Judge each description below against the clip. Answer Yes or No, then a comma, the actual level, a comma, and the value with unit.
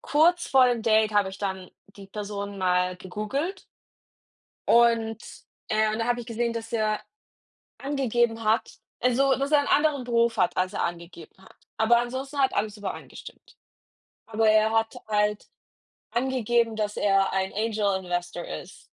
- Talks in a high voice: Yes, high, 220 Hz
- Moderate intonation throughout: Yes, average, 3.0 semitones